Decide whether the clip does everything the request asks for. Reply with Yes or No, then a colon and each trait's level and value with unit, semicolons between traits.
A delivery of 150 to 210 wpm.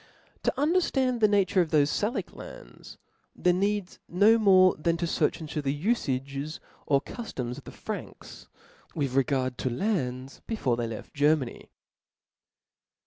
No: average, 140 wpm